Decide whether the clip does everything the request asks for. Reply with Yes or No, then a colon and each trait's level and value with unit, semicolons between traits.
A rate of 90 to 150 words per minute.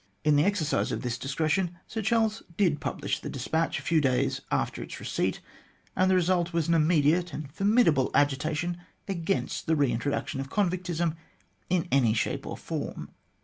No: average, 175 wpm